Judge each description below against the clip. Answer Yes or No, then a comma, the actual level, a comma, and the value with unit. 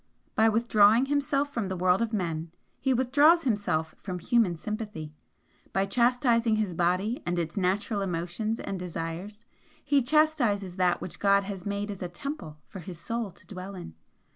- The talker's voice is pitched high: Yes, high, 205 Hz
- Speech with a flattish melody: No, average, 4.6 semitones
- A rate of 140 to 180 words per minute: Yes, average, 165 wpm